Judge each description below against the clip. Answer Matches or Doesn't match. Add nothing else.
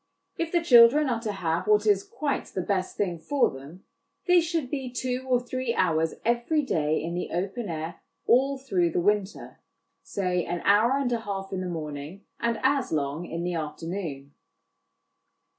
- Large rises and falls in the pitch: Matches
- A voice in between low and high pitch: Doesn't match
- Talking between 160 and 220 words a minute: Matches